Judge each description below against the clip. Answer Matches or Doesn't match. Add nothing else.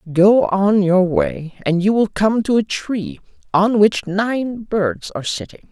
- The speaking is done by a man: Matches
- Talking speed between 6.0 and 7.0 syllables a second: Doesn't match